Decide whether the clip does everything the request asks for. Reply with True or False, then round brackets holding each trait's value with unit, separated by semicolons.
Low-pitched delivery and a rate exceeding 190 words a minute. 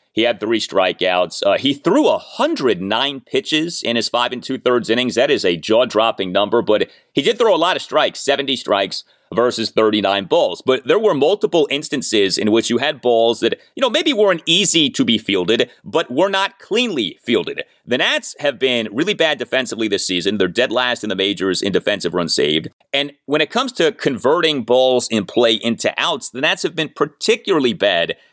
True (130 Hz; 200 wpm)